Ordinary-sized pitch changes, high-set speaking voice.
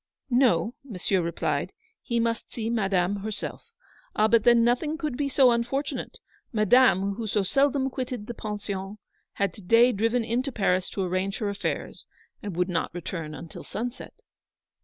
Yes: average, 4.0 semitones; high, 220 Hz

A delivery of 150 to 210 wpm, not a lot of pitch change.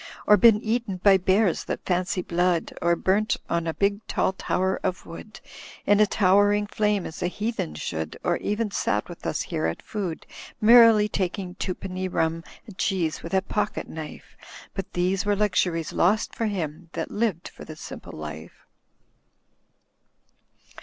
No: average, 160 wpm; average, 3.4 semitones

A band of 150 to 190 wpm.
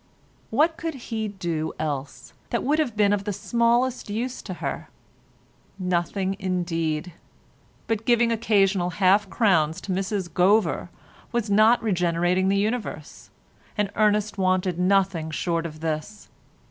No: slow, 135 wpm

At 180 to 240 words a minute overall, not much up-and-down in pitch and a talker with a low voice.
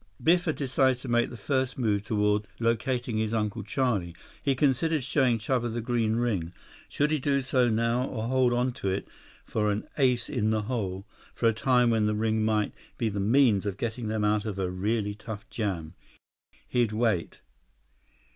No: average, 185 wpm; average, 3.1 semitones; low, 115 Hz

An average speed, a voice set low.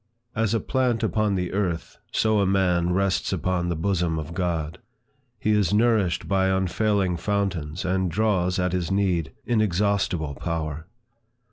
Yes: average, 145 wpm; very low, 95 Hz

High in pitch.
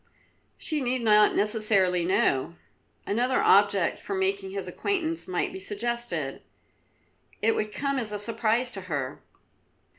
Yes: high, 225 Hz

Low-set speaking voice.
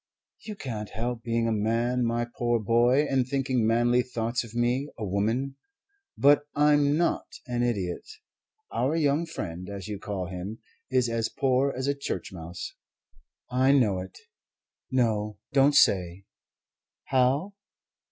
Yes: low, 120 Hz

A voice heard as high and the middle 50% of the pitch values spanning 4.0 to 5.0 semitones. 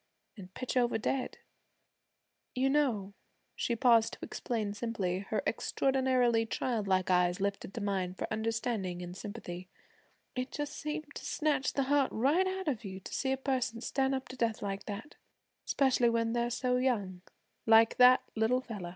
Yes: high, 230 Hz; average, 4.5 semitones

